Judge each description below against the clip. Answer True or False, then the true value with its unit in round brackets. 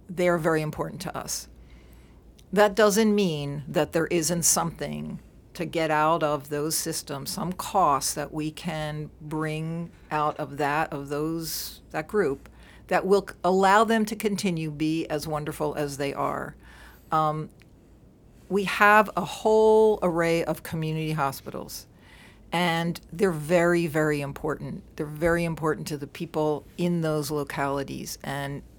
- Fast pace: False (140 wpm)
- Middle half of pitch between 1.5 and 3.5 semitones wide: True (2.7 semitones)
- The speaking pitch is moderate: True (155 Hz)